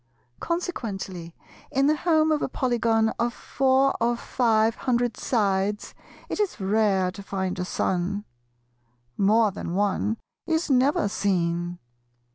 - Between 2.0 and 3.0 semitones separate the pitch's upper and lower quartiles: No, average, 5.3 semitones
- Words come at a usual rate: No, slow, 125 wpm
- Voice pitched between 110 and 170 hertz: No, high, 220 Hz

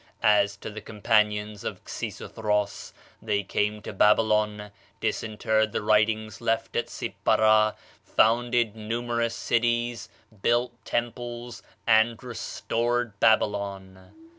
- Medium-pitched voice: No, low, 110 Hz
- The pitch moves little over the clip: Yes, narrow, 2.0 semitones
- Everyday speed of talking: No, slow, 100 wpm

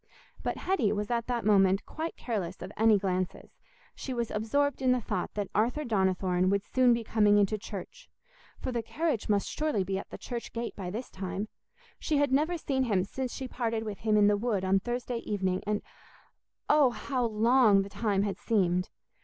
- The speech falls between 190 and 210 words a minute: Yes, average, 195 wpm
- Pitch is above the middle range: Yes, high, 215 Hz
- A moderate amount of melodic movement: Yes, average, 4.1 semitones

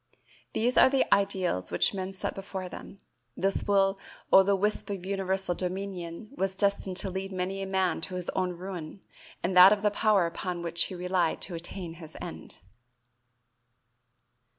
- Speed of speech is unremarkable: Yes, average, 170 wpm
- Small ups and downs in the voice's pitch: Yes, narrow, 1.6 semitones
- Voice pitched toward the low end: No, high, 190 Hz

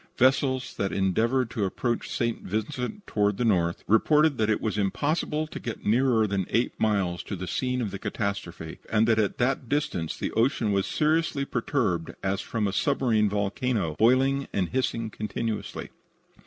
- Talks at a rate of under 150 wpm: No, average, 170 wpm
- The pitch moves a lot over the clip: No, average, 4.4 semitones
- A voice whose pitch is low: Yes, low, 110 Hz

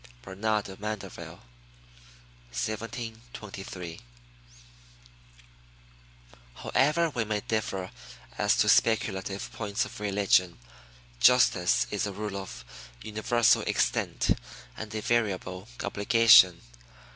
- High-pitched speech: No, low, 105 Hz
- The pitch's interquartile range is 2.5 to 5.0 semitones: Yes, average, 2.8 semitones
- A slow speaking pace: Yes, slow, 85 wpm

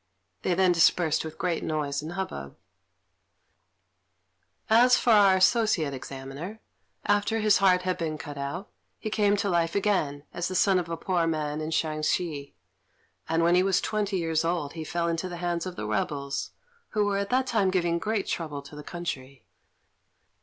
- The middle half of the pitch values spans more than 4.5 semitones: No, average, 4.0 semitones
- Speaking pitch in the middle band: Yes, medium, 170 Hz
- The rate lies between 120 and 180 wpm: Yes, average, 175 wpm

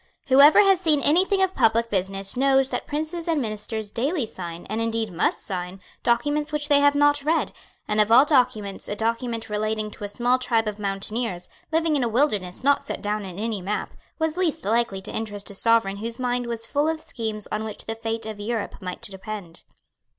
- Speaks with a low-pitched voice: No, high, 230 Hz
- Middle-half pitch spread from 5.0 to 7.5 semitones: Yes, wide, 5.5 semitones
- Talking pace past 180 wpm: Yes, average, 200 wpm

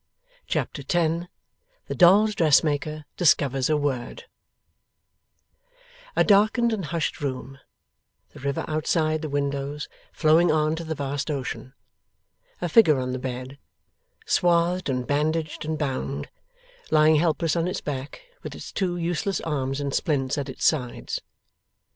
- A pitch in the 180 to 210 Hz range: No, medium, 155 Hz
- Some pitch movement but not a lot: Yes, average, 3.3 semitones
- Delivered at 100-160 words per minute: Yes, slow, 135 wpm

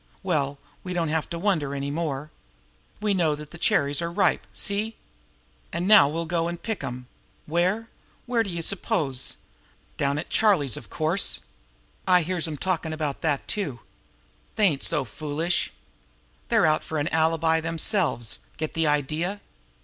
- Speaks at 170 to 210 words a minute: No, average, 160 wpm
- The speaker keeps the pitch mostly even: No, average, 3.7 semitones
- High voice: No, medium, 160 Hz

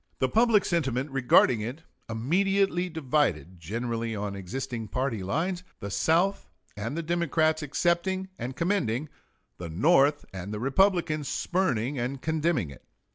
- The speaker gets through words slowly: Yes, slow, 130 wpm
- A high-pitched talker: No, low, 135 Hz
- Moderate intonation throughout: No, wide, 7.2 semitones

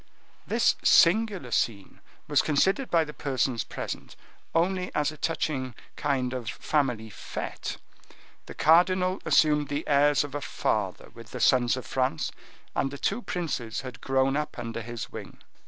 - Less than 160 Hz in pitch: Yes, medium, 140 Hz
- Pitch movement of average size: Yes, average, 4.4 semitones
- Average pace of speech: Yes, average, 155 wpm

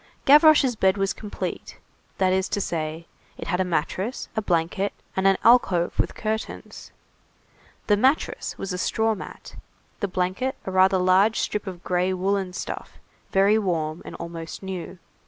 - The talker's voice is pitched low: No, high, 190 Hz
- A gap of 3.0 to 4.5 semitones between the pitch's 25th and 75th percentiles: No, narrow, 2.6 semitones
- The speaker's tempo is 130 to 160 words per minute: Yes, average, 155 wpm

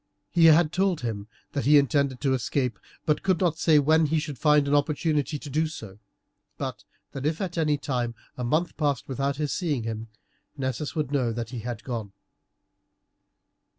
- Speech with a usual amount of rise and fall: Yes, average, 3.8 semitones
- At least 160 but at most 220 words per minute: Yes, average, 185 wpm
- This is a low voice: No, medium, 145 Hz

